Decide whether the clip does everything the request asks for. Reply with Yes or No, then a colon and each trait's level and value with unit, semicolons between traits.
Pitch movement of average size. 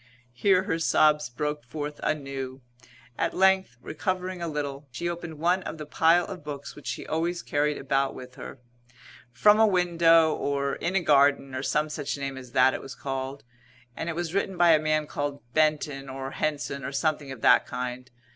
Yes: average, 3.5 semitones